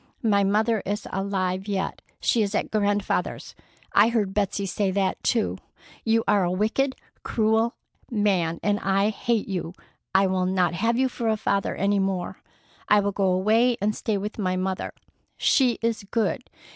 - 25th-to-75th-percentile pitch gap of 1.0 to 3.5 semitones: Yes, narrow, 2.5 semitones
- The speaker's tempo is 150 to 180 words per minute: Yes, average, 170 wpm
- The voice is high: Yes, high, 205 Hz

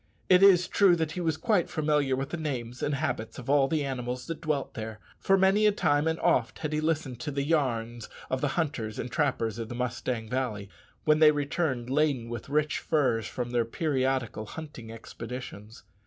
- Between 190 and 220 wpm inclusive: Yes, average, 195 wpm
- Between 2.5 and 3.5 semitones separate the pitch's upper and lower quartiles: No, average, 4.5 semitones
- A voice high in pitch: No, medium, 140 Hz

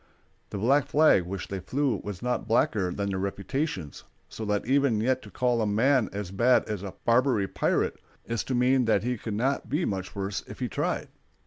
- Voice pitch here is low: Yes, low, 110 Hz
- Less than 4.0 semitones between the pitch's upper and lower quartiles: No, average, 4.4 semitones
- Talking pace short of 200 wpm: No, fast, 205 wpm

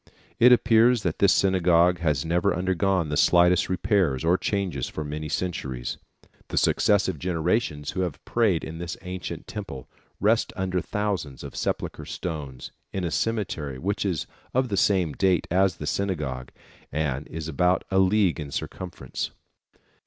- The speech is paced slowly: No, average, 155 wpm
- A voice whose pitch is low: Yes, very low, 90 Hz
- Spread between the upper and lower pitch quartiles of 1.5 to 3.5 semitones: No, average, 4.0 semitones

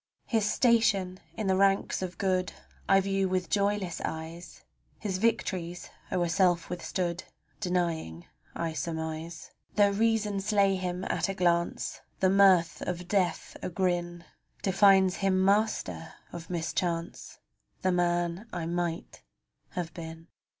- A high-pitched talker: No, medium, 180 Hz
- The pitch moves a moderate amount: No, narrow, 2.2 semitones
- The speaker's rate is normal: No, slow, 130 wpm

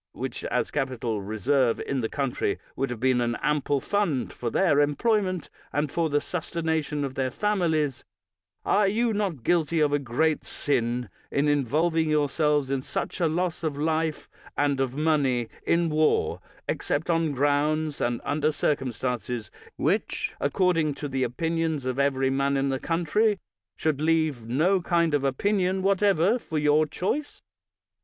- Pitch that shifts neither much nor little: Yes, average, 3.7 semitones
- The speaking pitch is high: No, medium, 150 Hz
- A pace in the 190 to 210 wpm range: No, average, 155 wpm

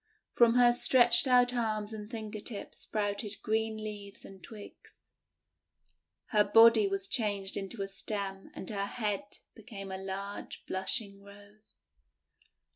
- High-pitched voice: Yes, high, 210 Hz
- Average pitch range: No, narrow, 2.1 semitones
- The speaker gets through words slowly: Yes, slow, 130 wpm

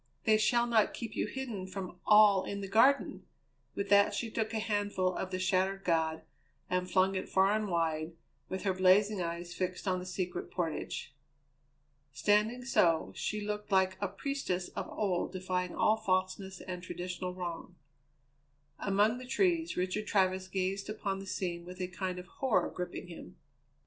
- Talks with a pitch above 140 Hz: Yes, high, 190 Hz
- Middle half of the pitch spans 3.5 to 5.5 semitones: No, narrow, 2.5 semitones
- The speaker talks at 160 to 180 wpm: Yes, average, 170 wpm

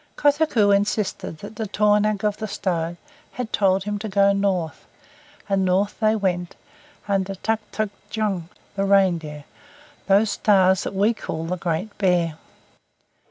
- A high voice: Yes, high, 200 Hz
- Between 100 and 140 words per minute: Yes, slow, 135 wpm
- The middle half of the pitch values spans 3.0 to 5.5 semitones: No, narrow, 2.4 semitones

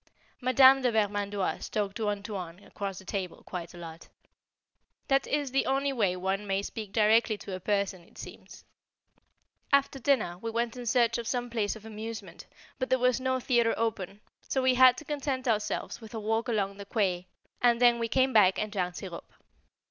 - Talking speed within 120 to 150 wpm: No, average, 190 wpm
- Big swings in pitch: No, average, 4.1 semitones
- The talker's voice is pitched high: Yes, high, 220 Hz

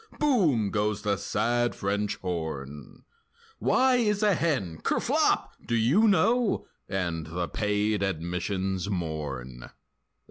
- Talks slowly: Yes, slow, 110 wpm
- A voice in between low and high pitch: No, low, 100 Hz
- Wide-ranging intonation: Yes, wide, 6.4 semitones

